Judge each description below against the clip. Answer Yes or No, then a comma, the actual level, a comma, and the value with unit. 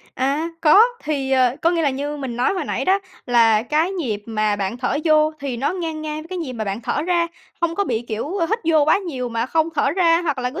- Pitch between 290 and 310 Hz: Yes, very high, 295 Hz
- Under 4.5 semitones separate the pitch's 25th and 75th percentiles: No, average, 5.2 semitones